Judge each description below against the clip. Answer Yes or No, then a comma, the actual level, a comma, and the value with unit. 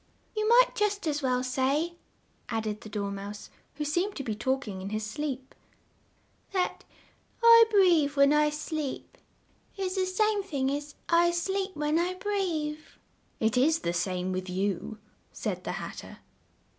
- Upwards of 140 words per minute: Yes, average, 160 wpm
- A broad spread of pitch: Yes, wide, 8.7 semitones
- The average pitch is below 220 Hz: No, very high, 295 Hz